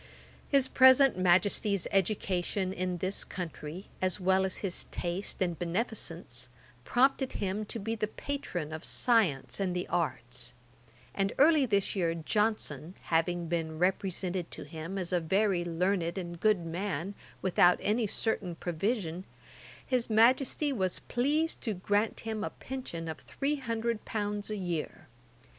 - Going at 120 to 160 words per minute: Yes, average, 145 wpm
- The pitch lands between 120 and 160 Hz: No, high, 190 Hz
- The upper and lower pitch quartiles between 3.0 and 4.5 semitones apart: Yes, average, 4.2 semitones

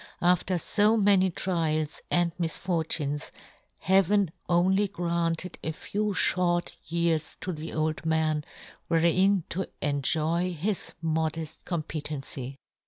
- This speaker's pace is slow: Yes, slow, 105 wpm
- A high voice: No, medium, 170 Hz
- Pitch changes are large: No, narrow, 2.6 semitones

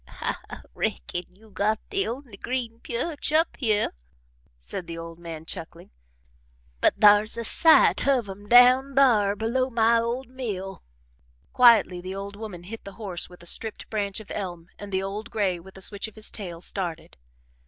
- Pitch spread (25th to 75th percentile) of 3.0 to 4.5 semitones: Yes, average, 4.0 semitones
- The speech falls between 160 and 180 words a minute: Yes, average, 175 wpm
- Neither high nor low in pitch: No, high, 205 Hz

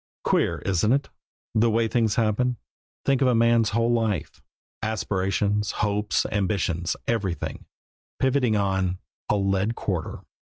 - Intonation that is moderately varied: Yes, average, 3.0 semitones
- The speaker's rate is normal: No, slow, 125 wpm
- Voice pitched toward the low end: Yes, low, 105 Hz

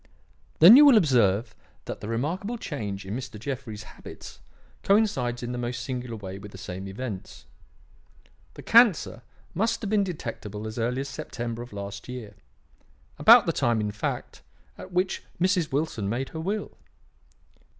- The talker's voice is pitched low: Yes, low, 125 Hz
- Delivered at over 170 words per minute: No, average, 160 wpm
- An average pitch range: No, wide, 8.5 semitones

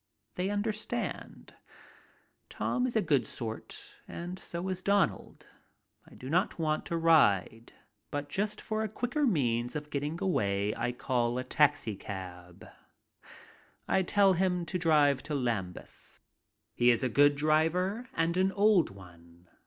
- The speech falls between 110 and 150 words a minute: Yes, average, 140 wpm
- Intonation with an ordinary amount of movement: No, wide, 8.0 semitones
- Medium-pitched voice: Yes, medium, 155 Hz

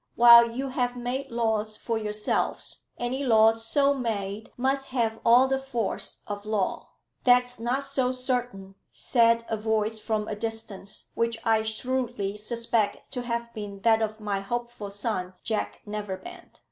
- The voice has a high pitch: Yes, high, 230 Hz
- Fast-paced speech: No, average, 150 wpm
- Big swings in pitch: No, narrow, 2.6 semitones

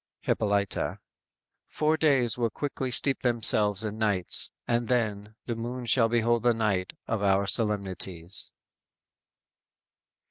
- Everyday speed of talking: No, slow, 120 wpm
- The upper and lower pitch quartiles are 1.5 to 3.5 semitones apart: Yes, average, 2.9 semitones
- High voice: No, low, 110 Hz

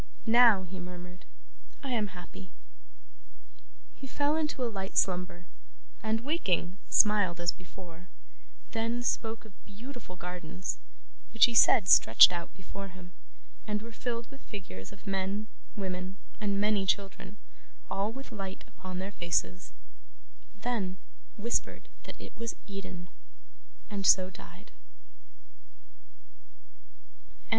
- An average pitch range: Yes, average, 3.6 semitones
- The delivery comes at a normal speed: No, slow, 120 wpm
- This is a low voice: No, high, 195 Hz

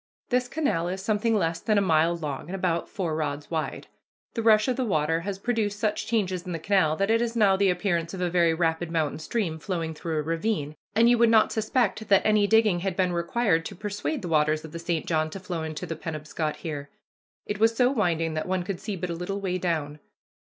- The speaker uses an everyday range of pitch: Yes, average, 4.5 semitones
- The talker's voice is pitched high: No, medium, 180 Hz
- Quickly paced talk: Yes, fast, 235 wpm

